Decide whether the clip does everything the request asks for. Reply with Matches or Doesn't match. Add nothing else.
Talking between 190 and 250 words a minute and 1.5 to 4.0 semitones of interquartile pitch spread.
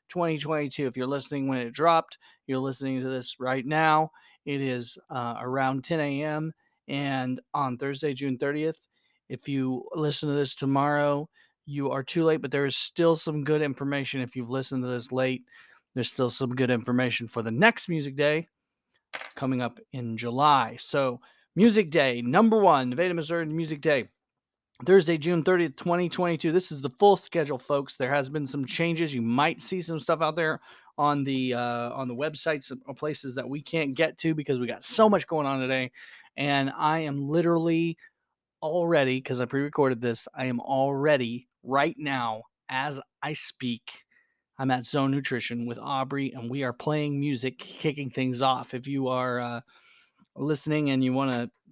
Doesn't match